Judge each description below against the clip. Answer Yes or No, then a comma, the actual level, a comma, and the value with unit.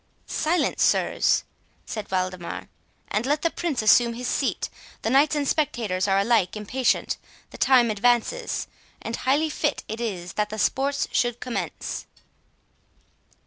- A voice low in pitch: No, high, 240 Hz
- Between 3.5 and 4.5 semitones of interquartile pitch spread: No, average, 4.9 semitones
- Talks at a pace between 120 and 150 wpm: Yes, average, 140 wpm